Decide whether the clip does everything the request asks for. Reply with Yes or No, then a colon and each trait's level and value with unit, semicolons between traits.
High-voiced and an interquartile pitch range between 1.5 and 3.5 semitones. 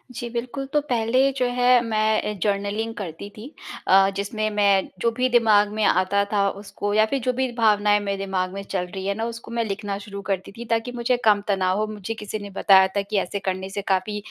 Yes: high, 210 Hz; narrow, 2.5 semitones